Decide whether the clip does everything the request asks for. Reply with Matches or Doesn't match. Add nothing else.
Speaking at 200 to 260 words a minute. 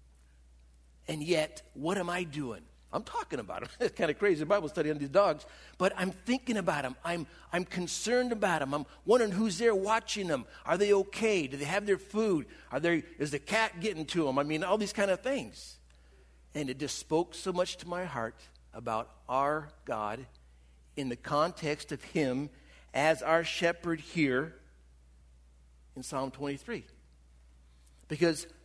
Doesn't match